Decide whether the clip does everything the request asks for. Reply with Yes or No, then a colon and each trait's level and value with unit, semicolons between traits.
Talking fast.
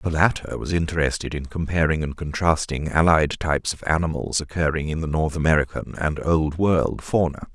No: average, 165 wpm